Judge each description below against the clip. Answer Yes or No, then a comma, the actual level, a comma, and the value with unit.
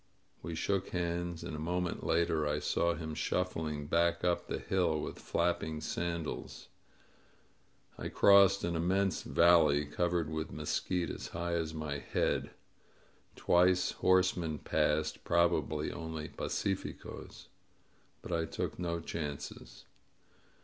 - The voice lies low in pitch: Yes, very low, 85 Hz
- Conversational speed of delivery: No, slow, 125 wpm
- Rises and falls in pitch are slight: Yes, narrow, 2.0 semitones